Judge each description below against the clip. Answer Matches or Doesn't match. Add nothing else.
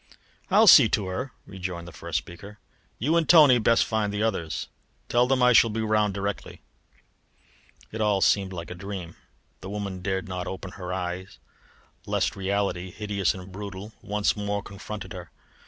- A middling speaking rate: Matches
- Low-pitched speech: Matches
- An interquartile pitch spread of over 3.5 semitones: Doesn't match